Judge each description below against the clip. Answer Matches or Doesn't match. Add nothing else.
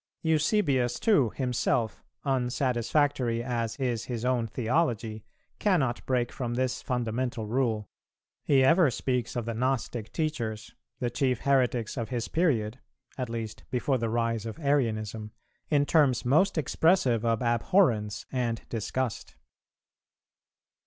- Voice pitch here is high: Doesn't match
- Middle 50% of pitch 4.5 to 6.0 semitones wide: Doesn't match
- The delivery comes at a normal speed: Doesn't match